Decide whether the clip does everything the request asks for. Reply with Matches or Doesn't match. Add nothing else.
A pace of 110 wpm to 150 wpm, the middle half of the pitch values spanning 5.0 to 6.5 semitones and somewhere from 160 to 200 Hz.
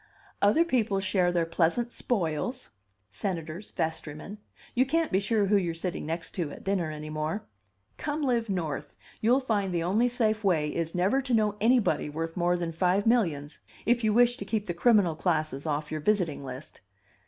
Doesn't match